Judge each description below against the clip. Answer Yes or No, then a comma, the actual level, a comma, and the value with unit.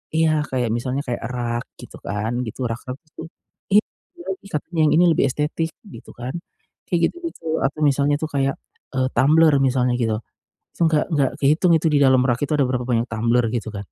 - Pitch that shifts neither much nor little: Yes, average, 4.2 semitones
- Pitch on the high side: No, low, 135 Hz